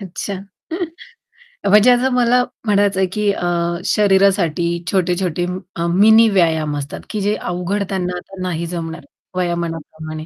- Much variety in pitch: No, average, 3.2 semitones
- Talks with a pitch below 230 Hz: Yes, medium, 185 Hz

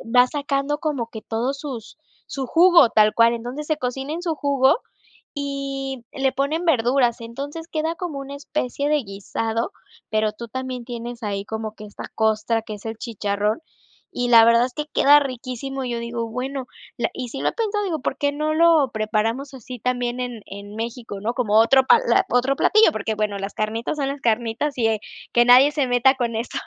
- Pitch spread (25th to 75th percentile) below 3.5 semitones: No, average, 3.8 semitones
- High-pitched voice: Yes, very high, 250 Hz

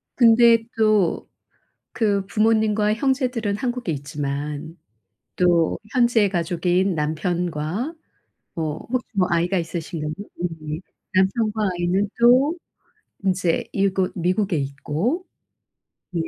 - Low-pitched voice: No, high, 190 Hz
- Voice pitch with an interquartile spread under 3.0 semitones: No, average, 5.1 semitones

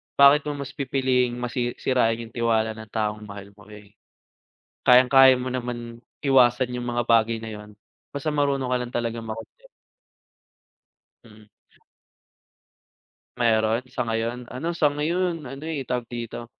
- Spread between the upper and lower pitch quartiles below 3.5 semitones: Yes, average, 2.8 semitones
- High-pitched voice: No, low, 120 Hz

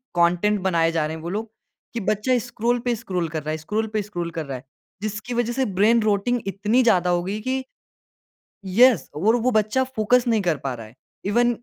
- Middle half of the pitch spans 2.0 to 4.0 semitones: No, wide, 5.5 semitones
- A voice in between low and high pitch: No, high, 210 Hz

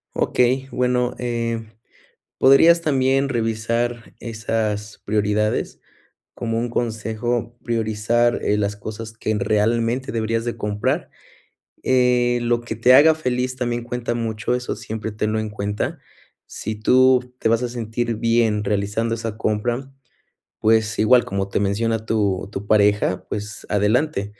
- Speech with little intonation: Yes, narrow, 2.3 semitones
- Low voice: Yes, low, 115 Hz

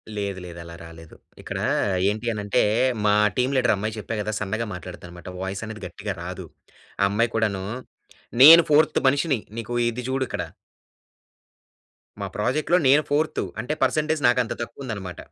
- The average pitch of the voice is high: No, low, 110 Hz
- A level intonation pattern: No, average, 5.0 semitones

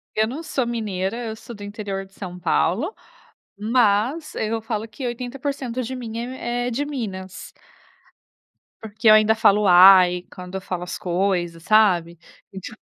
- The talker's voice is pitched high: Yes, high, 215 Hz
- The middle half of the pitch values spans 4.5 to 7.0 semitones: No, average, 4.0 semitones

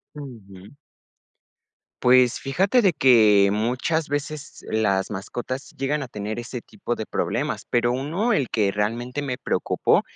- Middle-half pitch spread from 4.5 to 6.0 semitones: Yes, average, 5.0 semitones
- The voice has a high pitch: No, low, 125 Hz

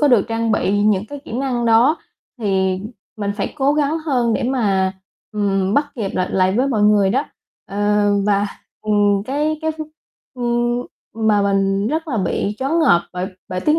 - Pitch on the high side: Yes, high, 215 Hz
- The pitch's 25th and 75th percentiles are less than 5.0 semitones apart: No, wide, 5.4 semitones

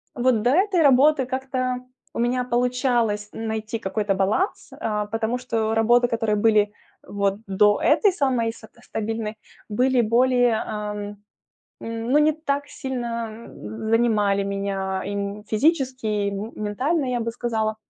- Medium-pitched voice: No, high, 225 Hz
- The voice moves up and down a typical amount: Yes, average, 3.3 semitones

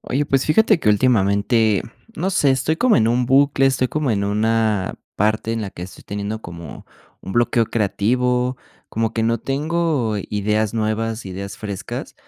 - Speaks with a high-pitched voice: No, low, 115 Hz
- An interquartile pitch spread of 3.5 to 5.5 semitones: Yes, average, 4.2 semitones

